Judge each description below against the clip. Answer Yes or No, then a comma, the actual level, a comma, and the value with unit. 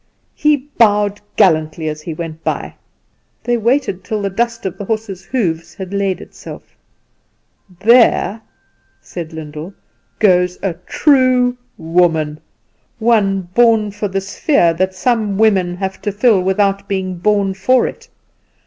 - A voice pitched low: No, high, 195 Hz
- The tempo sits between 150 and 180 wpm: No, slow, 135 wpm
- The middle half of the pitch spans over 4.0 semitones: No, average, 3.7 semitones